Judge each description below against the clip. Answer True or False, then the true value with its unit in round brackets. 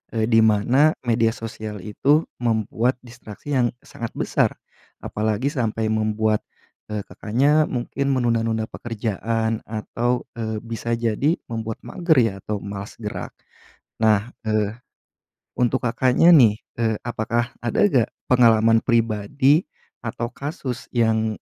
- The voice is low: True (115 Hz)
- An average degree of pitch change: False (2.2 semitones)